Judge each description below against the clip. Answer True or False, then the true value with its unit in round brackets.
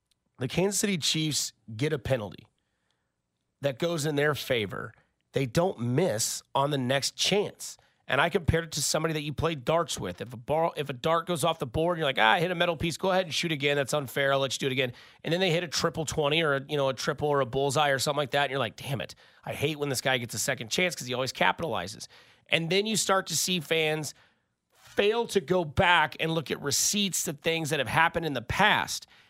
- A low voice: False (150 Hz)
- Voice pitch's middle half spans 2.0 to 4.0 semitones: True (3.7 semitones)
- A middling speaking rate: False (245 wpm)